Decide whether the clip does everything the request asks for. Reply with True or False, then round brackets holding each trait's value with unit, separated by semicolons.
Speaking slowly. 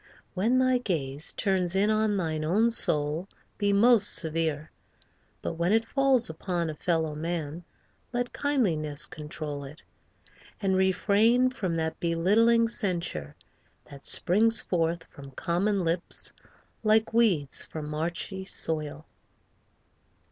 True (120 wpm)